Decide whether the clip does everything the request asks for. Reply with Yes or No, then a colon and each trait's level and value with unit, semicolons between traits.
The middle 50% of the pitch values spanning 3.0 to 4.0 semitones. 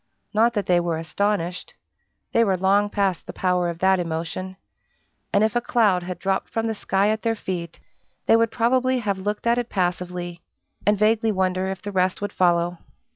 Yes: average, 3.3 semitones